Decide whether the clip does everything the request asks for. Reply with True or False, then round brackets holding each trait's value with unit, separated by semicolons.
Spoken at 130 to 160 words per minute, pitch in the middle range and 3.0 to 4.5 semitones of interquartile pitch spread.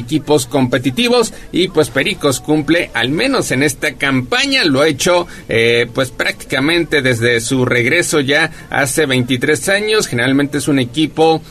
True (145 wpm; 150 Hz; 3.6 semitones)